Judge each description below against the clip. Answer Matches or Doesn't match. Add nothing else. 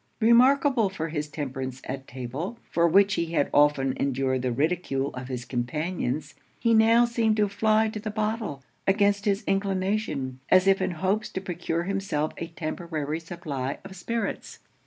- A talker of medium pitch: Matches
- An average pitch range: Doesn't match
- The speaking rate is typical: Matches